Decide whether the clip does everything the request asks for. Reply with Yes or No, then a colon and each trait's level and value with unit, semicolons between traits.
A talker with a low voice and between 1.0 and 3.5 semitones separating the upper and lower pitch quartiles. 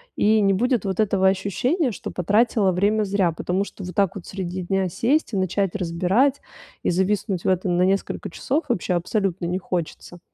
No: high, 195 Hz; average, 2.7 semitones